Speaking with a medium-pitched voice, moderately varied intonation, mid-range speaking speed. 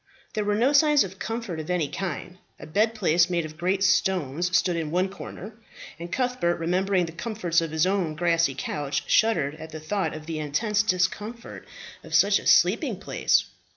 Yes: medium, 180 Hz; average, 4.2 semitones; average, 190 wpm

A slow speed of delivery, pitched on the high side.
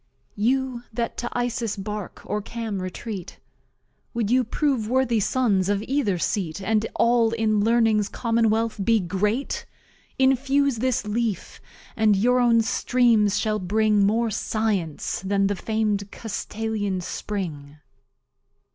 Yes: slow, 125 wpm; high, 220 Hz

